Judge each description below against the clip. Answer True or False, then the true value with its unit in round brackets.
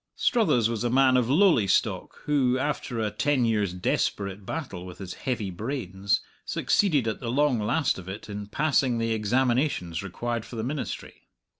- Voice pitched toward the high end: False (115 Hz)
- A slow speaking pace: False (170 wpm)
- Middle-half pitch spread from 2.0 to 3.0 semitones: False (4.8 semitones)